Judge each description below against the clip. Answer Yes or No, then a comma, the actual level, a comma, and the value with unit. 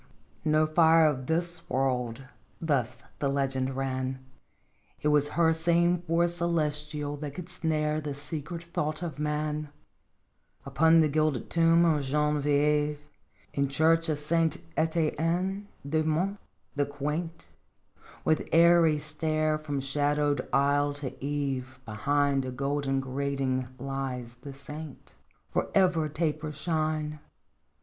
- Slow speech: Yes, slow, 130 wpm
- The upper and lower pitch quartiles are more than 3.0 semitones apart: No, narrow, 2.5 semitones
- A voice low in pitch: No, medium, 150 Hz